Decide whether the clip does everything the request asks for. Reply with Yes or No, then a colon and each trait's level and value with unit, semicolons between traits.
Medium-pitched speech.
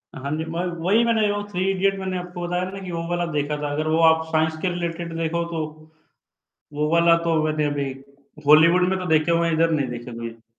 Yes: medium, 165 Hz